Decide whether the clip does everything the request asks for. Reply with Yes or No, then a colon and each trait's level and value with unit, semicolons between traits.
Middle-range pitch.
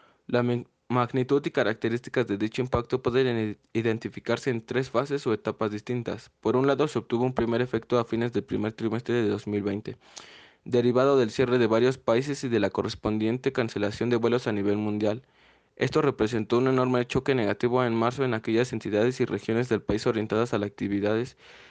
No: low, 120 Hz